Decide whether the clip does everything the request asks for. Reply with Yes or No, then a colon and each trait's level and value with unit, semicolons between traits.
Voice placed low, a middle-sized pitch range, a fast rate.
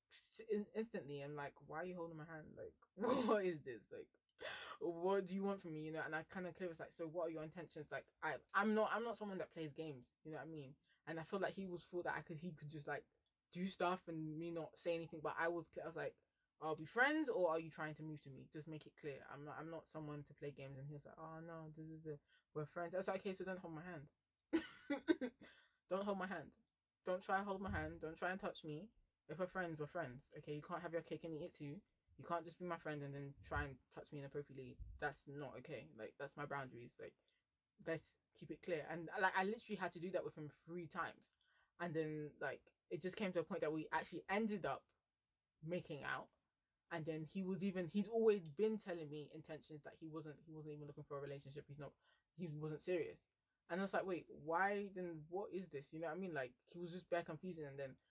No: medium, 165 Hz; average, 3.4 semitones; fast, 255 wpm